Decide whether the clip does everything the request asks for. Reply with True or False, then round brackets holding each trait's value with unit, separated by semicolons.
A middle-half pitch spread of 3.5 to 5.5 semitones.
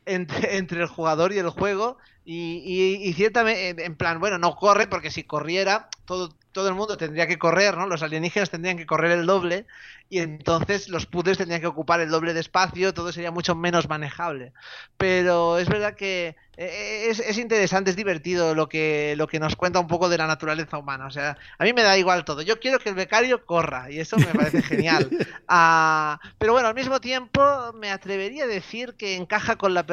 False (3.1 semitones)